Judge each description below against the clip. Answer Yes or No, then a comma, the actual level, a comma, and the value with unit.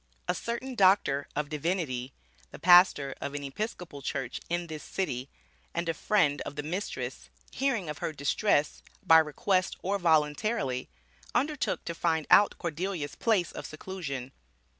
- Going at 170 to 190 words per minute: No, average, 145 wpm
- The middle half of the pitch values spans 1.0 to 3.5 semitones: No, average, 4.9 semitones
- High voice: No, medium, 165 Hz